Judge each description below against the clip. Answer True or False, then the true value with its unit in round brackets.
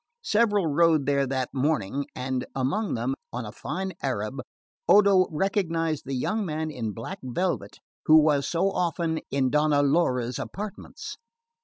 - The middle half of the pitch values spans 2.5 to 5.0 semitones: False (5.4 semitones)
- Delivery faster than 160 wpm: False (145 wpm)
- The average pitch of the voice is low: False (155 Hz)